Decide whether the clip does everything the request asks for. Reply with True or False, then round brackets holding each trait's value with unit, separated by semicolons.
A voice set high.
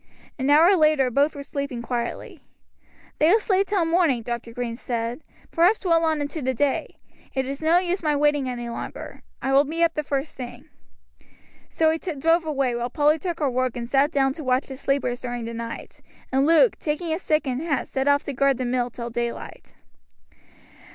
True (280 Hz)